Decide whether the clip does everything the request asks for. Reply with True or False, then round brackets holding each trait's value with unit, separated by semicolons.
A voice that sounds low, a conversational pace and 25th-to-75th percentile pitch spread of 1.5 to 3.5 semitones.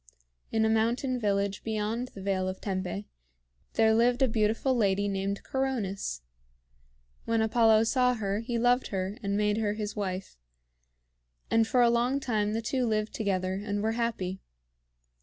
False (220 Hz; 160 wpm; 2.8 semitones)